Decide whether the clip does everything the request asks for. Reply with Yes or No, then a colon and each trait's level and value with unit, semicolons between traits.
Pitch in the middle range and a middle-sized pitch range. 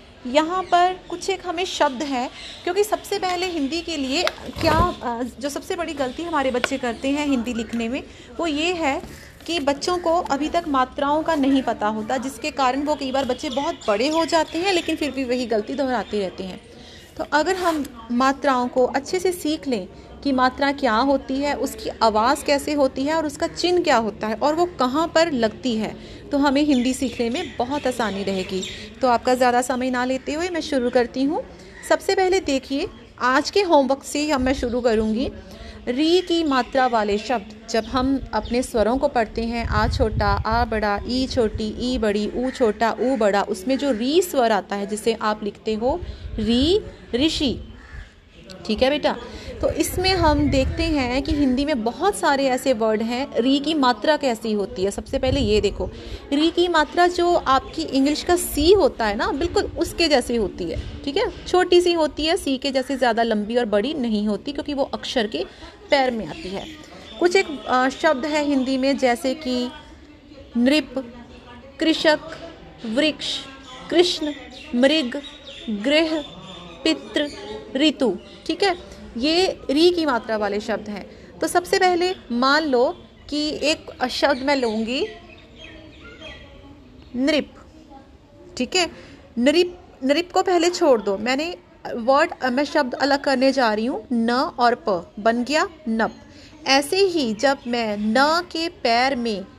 No: very high, 275 Hz; average, 4.6 semitones